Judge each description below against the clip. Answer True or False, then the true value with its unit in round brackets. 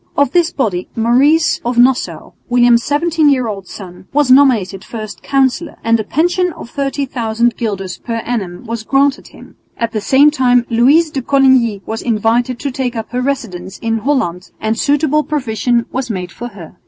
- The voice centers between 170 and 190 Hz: False (245 Hz)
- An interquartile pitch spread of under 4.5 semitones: True (4.0 semitones)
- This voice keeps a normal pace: True (175 wpm)